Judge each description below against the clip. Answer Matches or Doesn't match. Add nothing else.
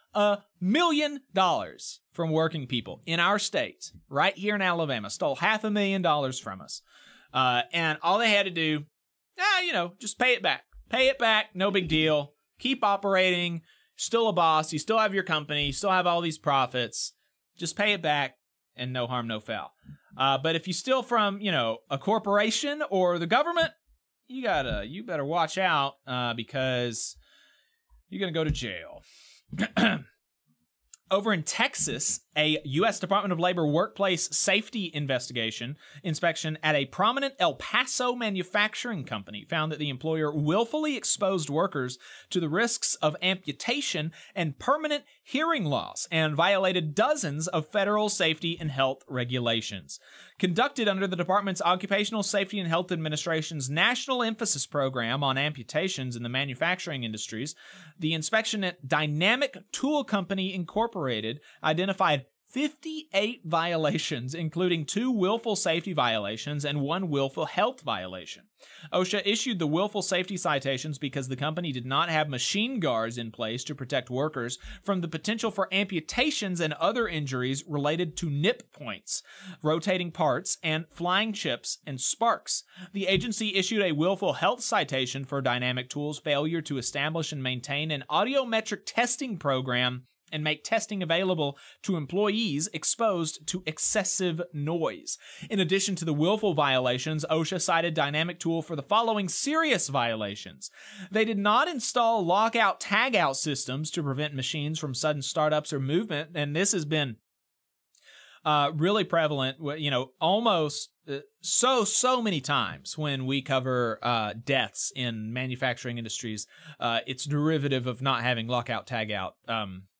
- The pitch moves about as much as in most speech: Doesn't match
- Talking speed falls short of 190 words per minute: Matches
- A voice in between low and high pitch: Matches